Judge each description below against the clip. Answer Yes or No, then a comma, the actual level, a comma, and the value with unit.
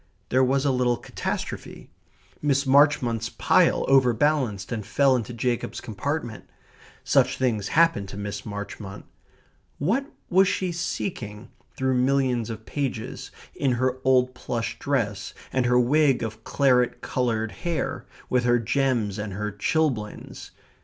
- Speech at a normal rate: No, slow, 130 wpm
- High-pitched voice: No, low, 125 Hz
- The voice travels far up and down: No, average, 3.8 semitones